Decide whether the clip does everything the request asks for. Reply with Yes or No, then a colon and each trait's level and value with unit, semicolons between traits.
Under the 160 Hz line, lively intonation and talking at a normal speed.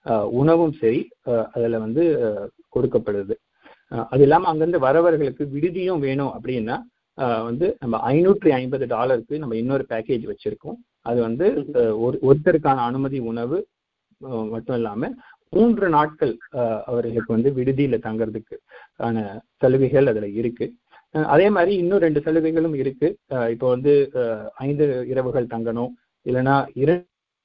Yes: low, 135 Hz; wide, 5.9 semitones; average, 115 wpm